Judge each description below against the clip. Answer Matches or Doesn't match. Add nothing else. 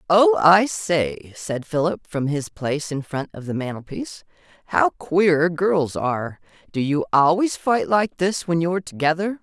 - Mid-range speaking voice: Matches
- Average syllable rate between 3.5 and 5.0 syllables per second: Matches